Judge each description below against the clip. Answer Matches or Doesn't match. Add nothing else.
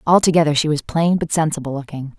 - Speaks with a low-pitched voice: Doesn't match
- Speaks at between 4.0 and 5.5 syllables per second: Doesn't match